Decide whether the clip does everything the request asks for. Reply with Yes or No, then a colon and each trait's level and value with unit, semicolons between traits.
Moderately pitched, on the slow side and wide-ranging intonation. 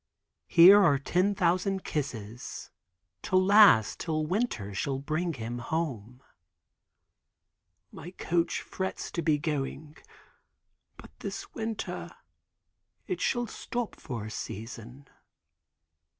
Yes: medium, 155 Hz; slow, 105 wpm; wide, 7.0 semitones